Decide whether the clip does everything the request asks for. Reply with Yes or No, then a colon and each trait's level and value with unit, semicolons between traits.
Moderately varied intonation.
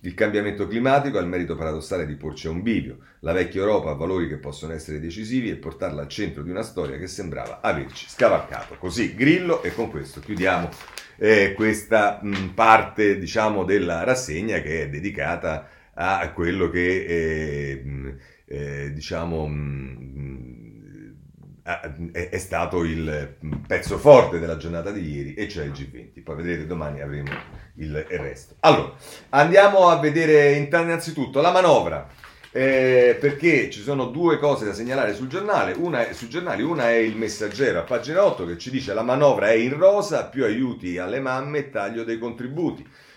No: wide, 8.6 semitones